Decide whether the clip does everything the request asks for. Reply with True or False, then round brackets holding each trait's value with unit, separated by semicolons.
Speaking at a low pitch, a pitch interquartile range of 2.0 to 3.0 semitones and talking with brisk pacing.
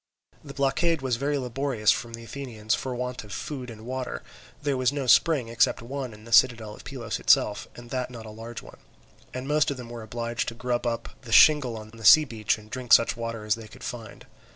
True (120 Hz; 2.6 semitones; 225 wpm)